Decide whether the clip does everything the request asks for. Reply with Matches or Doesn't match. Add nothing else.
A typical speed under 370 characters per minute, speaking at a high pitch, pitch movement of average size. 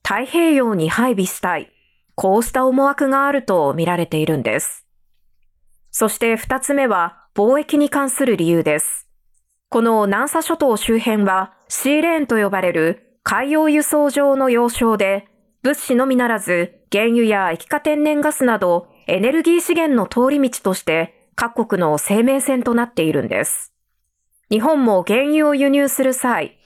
Doesn't match